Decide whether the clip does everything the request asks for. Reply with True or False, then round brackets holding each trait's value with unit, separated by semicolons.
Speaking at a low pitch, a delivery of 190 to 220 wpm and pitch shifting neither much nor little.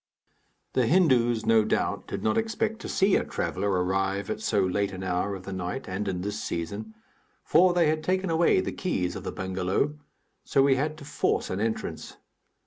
False (110 Hz; 195 wpm; 8.5 semitones)